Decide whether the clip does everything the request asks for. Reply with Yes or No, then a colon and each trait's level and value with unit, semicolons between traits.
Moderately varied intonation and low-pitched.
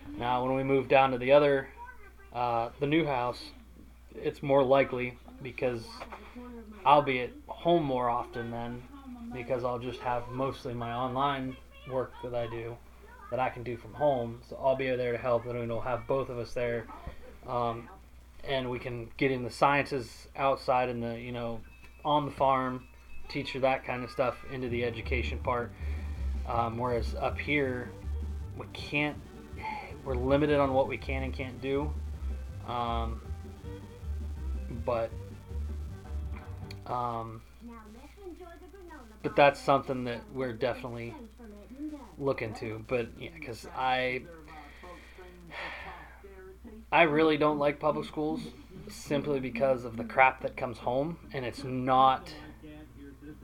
Yes: average, 3.5 semitones; low, 125 Hz